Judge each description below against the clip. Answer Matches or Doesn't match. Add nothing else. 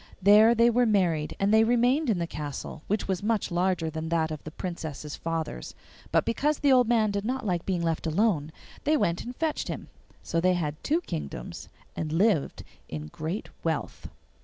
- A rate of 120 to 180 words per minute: Doesn't match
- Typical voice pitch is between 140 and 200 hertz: Matches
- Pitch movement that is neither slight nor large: Doesn't match